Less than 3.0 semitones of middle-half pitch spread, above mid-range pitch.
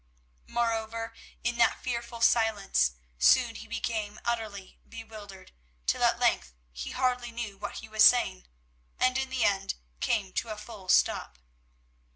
Yes: narrow, 2.6 semitones; high, 225 Hz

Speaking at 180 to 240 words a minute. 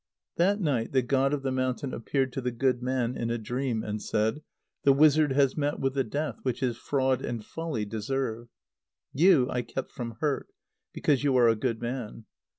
Yes: average, 195 wpm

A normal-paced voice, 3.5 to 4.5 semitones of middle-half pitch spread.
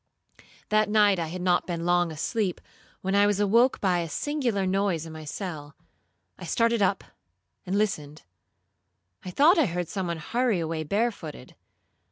Yes: average, 165 wpm; average, 4.1 semitones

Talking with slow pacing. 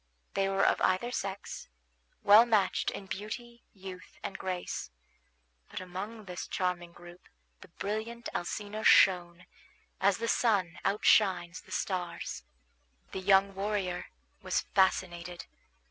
Yes: slow, 120 wpm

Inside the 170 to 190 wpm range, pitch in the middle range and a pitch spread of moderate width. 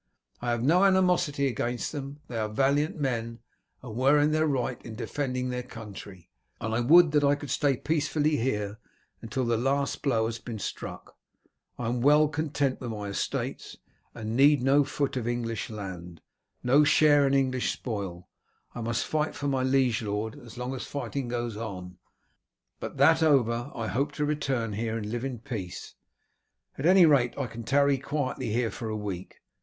No: average, 180 wpm; low, 125 Hz; average, 4.0 semitones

